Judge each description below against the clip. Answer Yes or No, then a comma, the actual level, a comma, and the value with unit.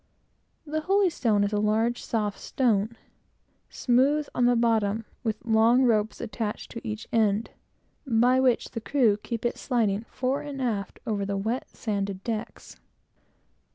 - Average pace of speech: Yes, average, 145 wpm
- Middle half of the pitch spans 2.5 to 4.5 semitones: Yes, average, 2.9 semitones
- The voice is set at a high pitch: Yes, high, 225 Hz